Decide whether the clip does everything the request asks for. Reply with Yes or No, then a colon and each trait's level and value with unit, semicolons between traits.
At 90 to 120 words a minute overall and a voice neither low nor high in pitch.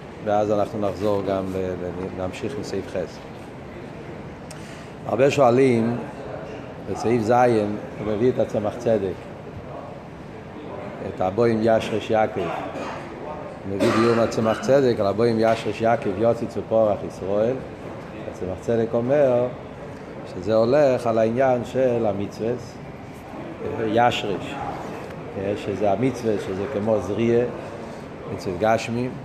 No: slow, 100 wpm; low, 115 Hz